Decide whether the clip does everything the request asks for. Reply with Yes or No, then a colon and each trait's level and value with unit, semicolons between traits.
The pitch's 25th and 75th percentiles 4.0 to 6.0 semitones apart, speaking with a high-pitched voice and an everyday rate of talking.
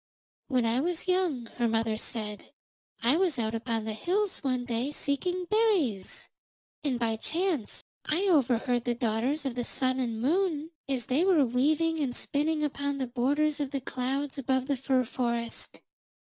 Yes: average, 4.4 semitones; very high, 265 Hz; average, 165 wpm